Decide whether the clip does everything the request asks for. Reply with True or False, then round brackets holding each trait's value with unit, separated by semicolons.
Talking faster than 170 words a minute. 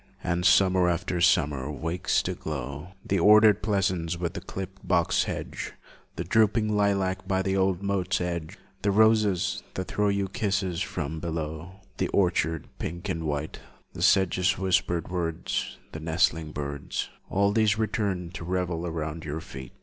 False (155 wpm)